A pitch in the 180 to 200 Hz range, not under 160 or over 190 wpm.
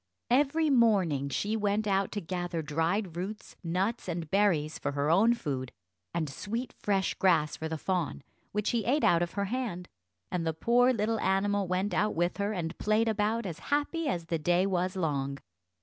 Yes: high, 190 Hz; average, 185 wpm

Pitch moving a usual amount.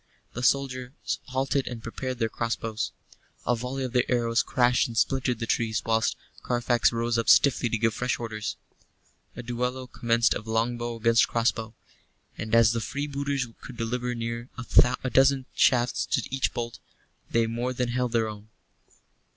No: narrow, 1.7 semitones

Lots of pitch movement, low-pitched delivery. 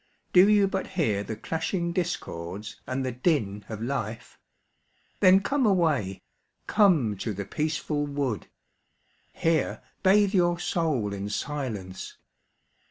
No: wide, 8.7 semitones; medium, 145 Hz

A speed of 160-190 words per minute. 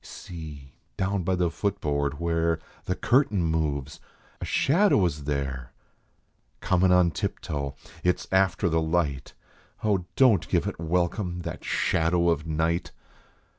No: average, 140 wpm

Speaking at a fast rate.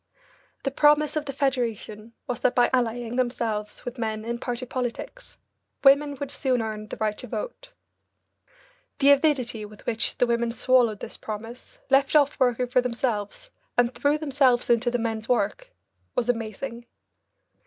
No: average, 155 wpm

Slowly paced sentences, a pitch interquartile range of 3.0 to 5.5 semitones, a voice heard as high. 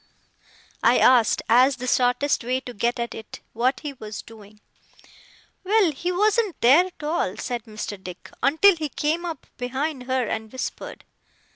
No: average, 160 wpm; average, 5.2 semitones; very high, 255 Hz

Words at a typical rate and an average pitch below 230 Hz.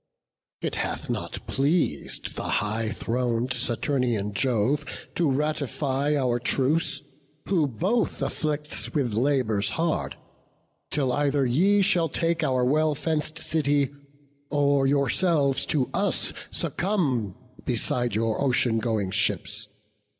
No: slow, 110 wpm; medium, 140 Hz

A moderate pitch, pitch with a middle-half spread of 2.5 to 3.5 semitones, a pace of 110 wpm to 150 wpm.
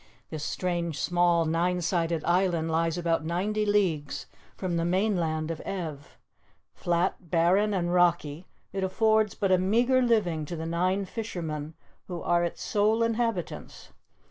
Yes: medium, 175 Hz; average, 2.9 semitones; average, 145 wpm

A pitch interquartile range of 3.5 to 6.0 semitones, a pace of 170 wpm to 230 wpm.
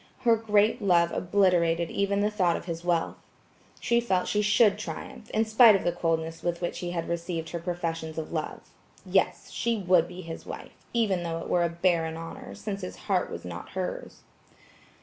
Yes: average, 3.8 semitones; average, 190 wpm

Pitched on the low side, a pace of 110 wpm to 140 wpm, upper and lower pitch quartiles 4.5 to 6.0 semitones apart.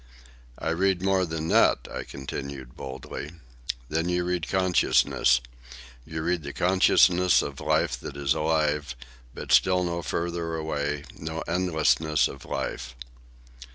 No: very low, 80 Hz; slow, 135 wpm; average, 3.5 semitones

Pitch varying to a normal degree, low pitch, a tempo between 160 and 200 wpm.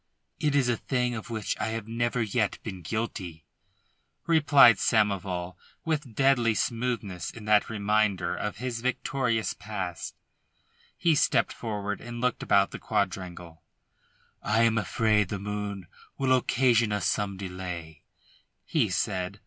No: average, 3.3 semitones; low, 110 Hz; slow, 135 wpm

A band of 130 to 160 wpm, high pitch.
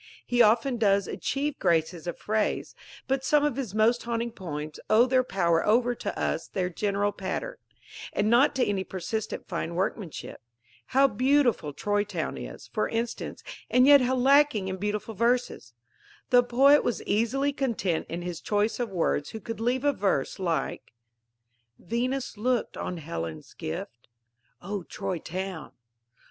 Yes: average, 155 wpm; high, 215 Hz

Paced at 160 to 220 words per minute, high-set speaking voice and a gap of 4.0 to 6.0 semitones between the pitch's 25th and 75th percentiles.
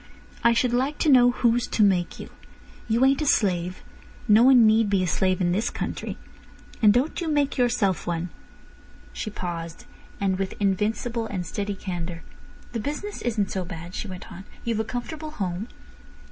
Yes: average, 175 wpm; high, 210 Hz; average, 4.8 semitones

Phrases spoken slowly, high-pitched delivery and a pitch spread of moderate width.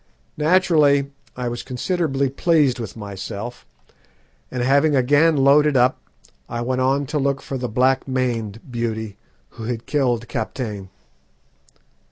No: slow, 130 wpm; low, 130 Hz; average, 3.1 semitones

